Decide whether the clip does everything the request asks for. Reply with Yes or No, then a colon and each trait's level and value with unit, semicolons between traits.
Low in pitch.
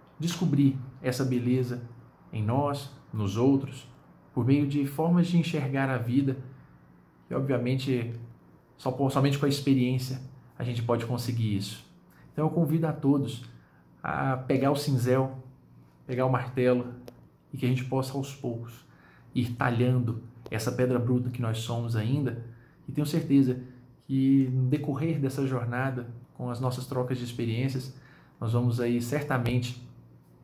Yes: low, 130 Hz